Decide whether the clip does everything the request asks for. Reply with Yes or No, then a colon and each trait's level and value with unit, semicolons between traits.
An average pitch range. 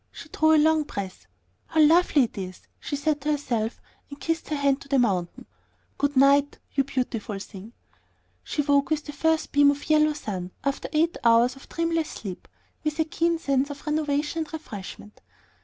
Yes: average, 4.3 semitones